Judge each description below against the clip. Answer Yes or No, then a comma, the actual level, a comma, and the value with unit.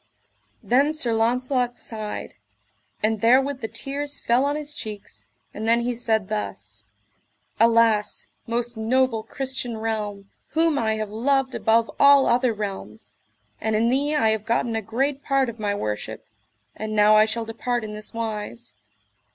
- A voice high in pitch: Yes, high, 230 Hz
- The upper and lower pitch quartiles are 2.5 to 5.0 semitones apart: Yes, average, 3.1 semitones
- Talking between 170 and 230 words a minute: No, average, 155 wpm